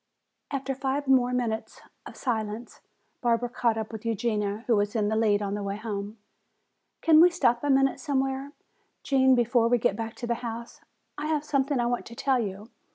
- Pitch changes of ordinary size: Yes, average, 3.5 semitones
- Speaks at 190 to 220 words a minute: Yes, average, 195 wpm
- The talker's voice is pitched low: No, high, 240 Hz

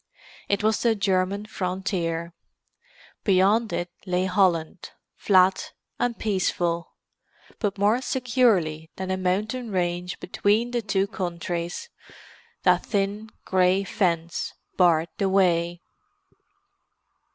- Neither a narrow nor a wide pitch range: Yes, average, 3.0 semitones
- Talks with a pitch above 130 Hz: Yes, high, 190 Hz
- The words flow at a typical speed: No, slow, 105 wpm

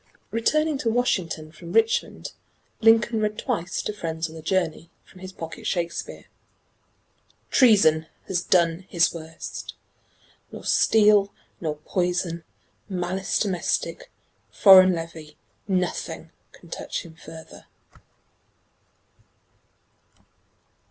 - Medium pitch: Yes, medium, 180 Hz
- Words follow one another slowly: Yes, slow, 100 wpm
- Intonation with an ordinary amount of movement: Yes, average, 4.2 semitones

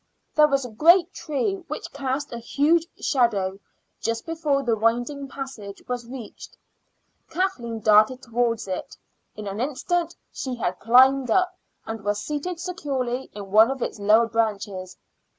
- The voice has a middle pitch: No, high, 245 Hz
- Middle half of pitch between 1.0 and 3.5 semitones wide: No, average, 4.6 semitones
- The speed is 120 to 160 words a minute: Yes, average, 150 wpm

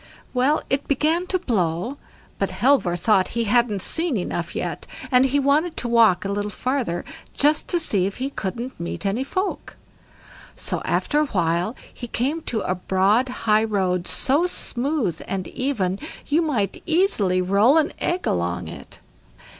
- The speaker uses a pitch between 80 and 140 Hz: No, high, 235 Hz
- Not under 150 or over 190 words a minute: Yes, average, 160 wpm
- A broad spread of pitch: Yes, wide, 6.9 semitones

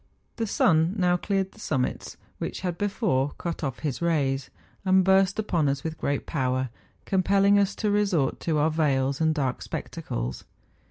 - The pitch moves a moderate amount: No, wide, 5.7 semitones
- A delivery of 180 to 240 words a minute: No, average, 165 wpm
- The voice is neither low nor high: Yes, medium, 165 Hz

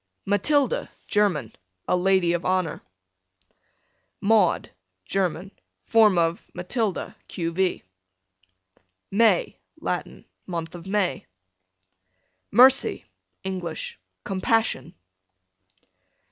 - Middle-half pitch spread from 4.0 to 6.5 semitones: No, average, 3.3 semitones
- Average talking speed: No, slow, 75 wpm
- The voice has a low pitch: No, high, 190 Hz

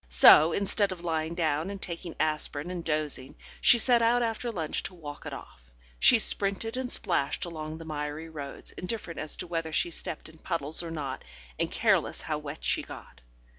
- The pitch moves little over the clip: No, average, 3.8 semitones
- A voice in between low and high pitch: Yes, medium, 165 Hz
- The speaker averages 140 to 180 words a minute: No, average, 190 wpm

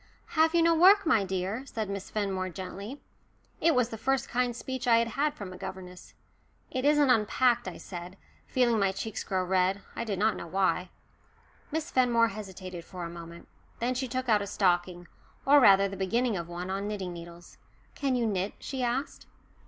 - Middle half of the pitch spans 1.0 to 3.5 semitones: No, average, 5.3 semitones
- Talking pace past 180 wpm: Yes, average, 190 wpm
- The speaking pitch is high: Yes, high, 210 Hz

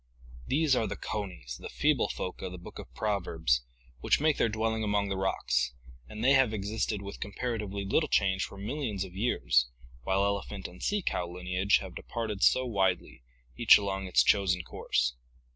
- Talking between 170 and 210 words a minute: Yes, average, 180 wpm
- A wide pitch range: No, average, 3.3 semitones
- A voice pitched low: Yes, low, 100 Hz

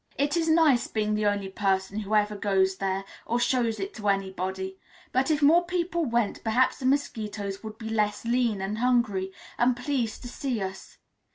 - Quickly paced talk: No, average, 185 wpm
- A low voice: No, high, 220 Hz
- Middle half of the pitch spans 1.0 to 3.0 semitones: No, average, 4.5 semitones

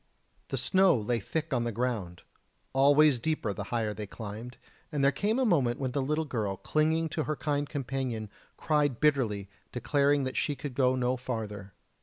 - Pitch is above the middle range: No, low, 130 Hz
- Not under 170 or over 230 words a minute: Yes, average, 180 wpm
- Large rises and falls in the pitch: No, average, 4.5 semitones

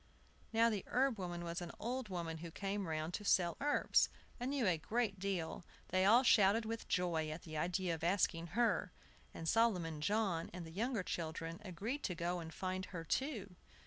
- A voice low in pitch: No, medium, 185 Hz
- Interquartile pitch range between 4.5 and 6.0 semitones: Yes, average, 4.8 semitones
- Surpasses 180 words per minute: Yes, average, 190 wpm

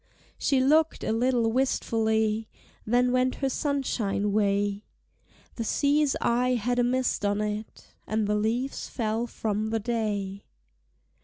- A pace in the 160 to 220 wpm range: No, slow, 135 wpm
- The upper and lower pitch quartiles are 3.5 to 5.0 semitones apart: No, average, 3.1 semitones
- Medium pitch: No, high, 225 Hz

